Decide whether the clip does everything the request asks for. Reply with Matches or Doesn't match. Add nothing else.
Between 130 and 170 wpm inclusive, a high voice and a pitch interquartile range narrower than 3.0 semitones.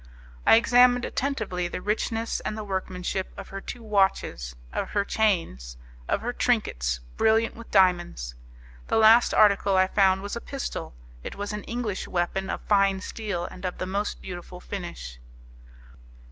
Doesn't match